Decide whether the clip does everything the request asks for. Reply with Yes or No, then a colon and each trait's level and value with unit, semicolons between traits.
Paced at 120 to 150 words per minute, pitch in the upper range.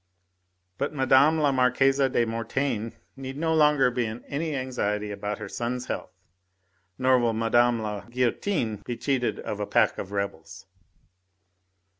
No: average, 145 wpm; low, 125 Hz